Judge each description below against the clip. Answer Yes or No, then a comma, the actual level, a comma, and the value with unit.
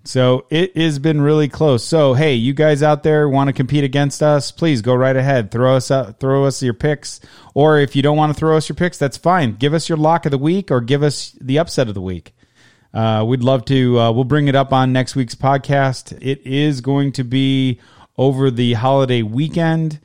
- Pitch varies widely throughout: No, average, 2.7 semitones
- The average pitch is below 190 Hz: Yes, medium, 140 Hz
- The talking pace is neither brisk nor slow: No, fast, 230 wpm